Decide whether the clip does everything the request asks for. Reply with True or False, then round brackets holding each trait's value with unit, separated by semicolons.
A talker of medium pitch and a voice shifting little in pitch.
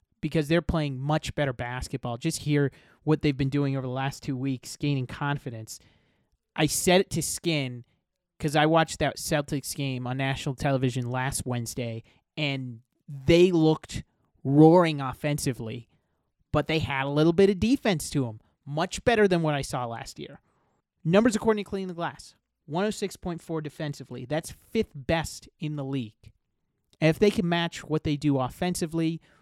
False (150 Hz; 3.8 semitones)